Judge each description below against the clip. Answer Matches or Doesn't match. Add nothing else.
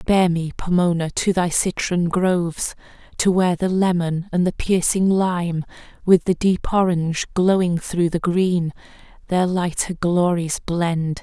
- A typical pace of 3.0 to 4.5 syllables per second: Matches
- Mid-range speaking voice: Matches